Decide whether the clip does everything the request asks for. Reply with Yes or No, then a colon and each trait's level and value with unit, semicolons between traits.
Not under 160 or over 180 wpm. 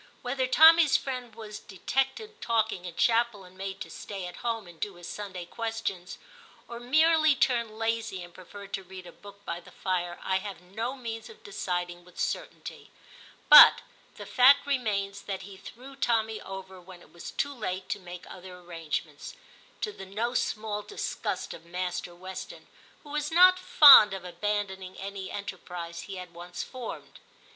Yes: average, 175 wpm